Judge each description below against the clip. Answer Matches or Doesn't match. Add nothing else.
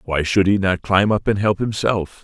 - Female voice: Doesn't match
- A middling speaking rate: Doesn't match